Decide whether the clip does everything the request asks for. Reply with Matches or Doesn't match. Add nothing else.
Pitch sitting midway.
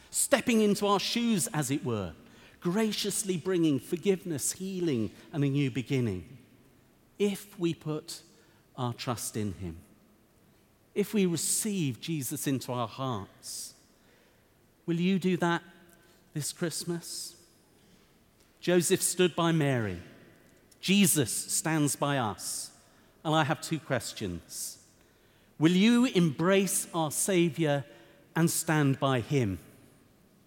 Matches